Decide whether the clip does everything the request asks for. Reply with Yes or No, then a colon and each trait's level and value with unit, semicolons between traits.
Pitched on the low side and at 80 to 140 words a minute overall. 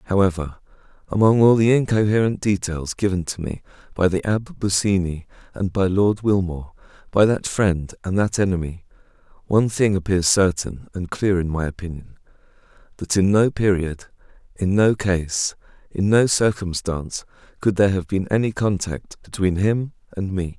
No: very low, 95 Hz; average, 150 wpm